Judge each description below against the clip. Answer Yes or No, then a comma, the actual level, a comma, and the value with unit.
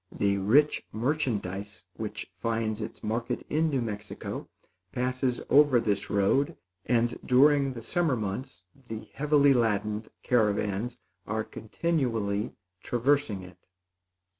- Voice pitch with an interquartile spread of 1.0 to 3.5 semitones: No, average, 4.6 semitones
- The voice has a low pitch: Yes, low, 115 Hz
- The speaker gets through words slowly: Yes, slow, 115 wpm